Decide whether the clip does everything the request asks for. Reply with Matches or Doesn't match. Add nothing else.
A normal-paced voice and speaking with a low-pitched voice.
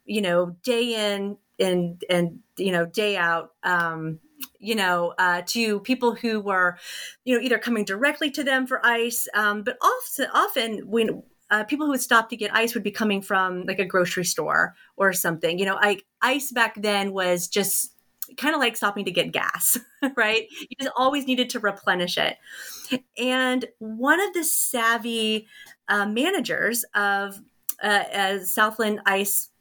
Doesn't match